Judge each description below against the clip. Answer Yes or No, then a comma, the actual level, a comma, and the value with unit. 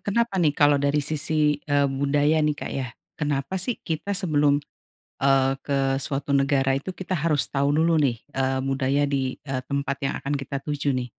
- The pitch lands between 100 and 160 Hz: Yes, medium, 140 Hz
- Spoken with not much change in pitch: Yes, narrow, 1.8 semitones